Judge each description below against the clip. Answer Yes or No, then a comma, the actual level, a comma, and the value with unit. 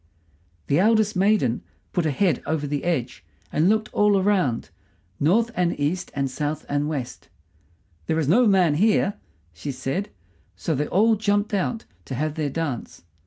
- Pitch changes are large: Yes, wide, 6.1 semitones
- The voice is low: No, medium, 165 Hz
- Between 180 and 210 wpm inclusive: No, average, 165 wpm